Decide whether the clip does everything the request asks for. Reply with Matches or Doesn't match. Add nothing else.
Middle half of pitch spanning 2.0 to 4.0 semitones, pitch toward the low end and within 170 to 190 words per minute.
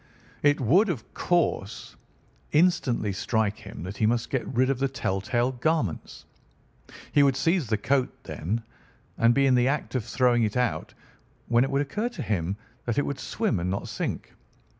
Doesn't match